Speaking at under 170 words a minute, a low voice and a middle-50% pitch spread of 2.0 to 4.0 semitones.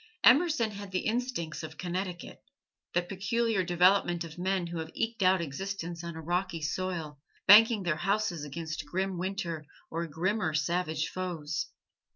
No: average, 150 wpm; medium, 180 Hz; average, 3.0 semitones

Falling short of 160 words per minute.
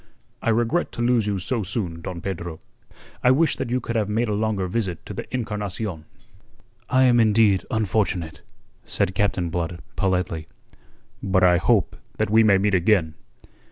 No: average, 165 wpm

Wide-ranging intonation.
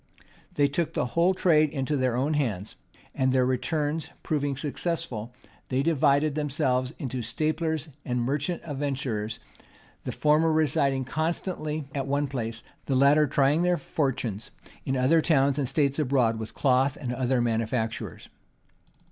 No: average, 3.2 semitones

